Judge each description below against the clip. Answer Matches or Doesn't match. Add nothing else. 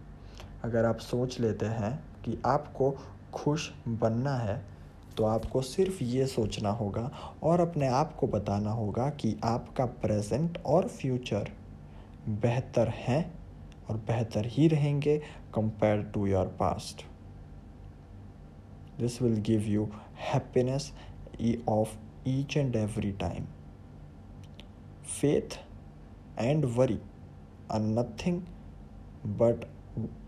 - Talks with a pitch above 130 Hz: Doesn't match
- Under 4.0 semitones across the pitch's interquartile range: Doesn't match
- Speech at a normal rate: Doesn't match